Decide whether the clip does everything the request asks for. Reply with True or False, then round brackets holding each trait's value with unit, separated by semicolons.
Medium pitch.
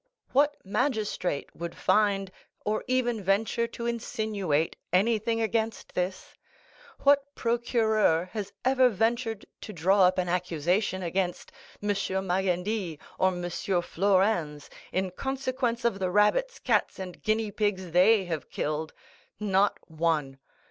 False (200 Hz)